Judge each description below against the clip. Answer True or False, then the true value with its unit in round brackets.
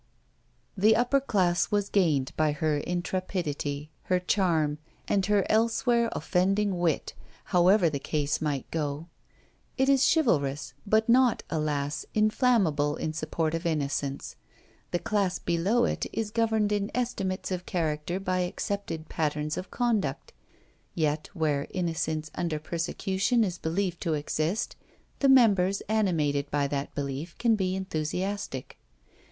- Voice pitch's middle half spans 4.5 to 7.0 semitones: True (5.1 semitones)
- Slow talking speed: True (130 wpm)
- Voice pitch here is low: False (175 Hz)